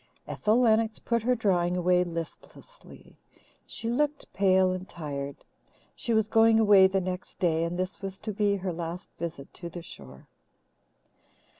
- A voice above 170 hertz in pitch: Yes, high, 190 Hz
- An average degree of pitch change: Yes, average, 4.1 semitones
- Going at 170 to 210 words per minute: No, average, 155 wpm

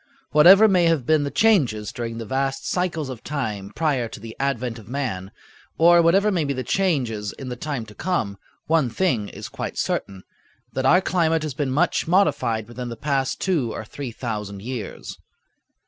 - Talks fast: No, average, 185 wpm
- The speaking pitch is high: No, low, 135 Hz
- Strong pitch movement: Yes, wide, 6.3 semitones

